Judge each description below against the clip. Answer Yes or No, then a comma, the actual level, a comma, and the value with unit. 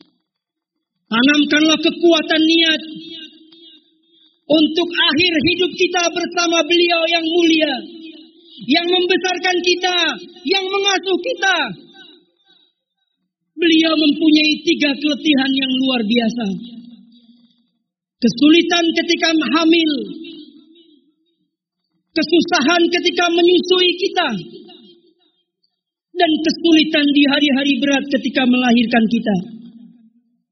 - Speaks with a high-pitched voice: Yes, very high, 315 Hz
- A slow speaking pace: Yes, slow, 75 wpm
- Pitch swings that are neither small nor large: Yes, average, 4.4 semitones